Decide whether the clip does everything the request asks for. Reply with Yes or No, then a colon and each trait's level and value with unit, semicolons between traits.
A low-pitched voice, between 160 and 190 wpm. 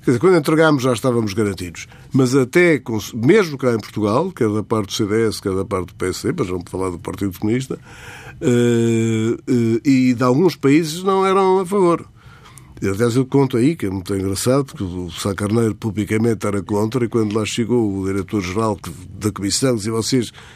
Yes: low, 115 Hz; average, 175 wpm